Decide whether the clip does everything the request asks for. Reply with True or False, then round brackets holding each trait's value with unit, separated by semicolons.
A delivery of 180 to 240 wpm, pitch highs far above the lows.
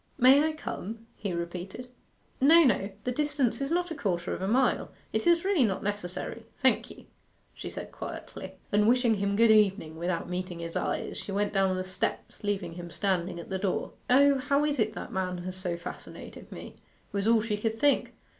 True (200 wpm; 5.7 semitones)